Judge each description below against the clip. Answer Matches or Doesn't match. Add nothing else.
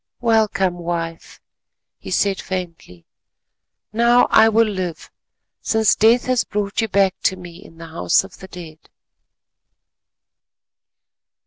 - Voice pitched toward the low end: Doesn't match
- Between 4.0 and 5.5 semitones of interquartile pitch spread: Matches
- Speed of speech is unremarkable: Doesn't match